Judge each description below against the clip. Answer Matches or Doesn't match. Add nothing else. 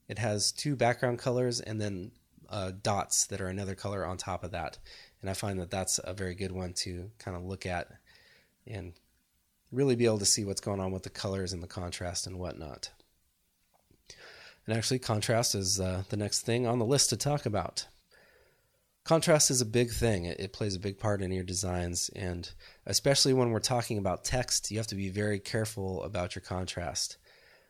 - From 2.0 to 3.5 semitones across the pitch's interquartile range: Doesn't match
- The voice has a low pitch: Matches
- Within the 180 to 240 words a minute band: Matches